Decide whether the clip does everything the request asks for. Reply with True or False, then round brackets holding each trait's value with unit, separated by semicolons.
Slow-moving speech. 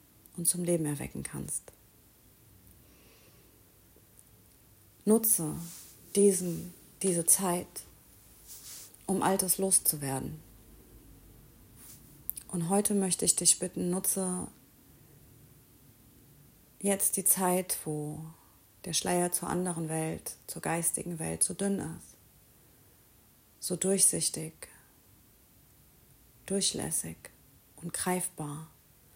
True (80 wpm)